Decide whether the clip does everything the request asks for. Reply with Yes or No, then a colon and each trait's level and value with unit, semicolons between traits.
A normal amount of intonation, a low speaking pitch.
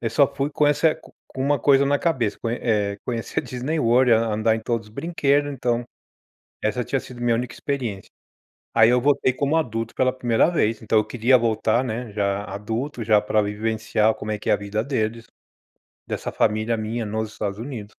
Yes: average, 3.3 semitones; low, 115 Hz